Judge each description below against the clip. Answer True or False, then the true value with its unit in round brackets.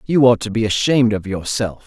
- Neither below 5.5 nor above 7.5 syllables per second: True (5.7 syllables/s)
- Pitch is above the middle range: False (110 Hz)